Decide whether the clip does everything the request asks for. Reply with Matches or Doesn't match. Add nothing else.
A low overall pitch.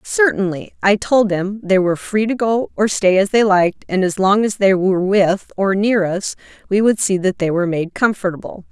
Doesn't match